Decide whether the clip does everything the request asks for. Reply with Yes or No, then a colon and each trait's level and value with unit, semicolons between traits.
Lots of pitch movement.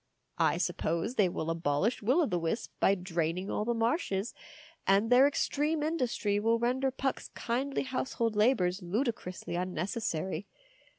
Yes: wide, 5.9 semitones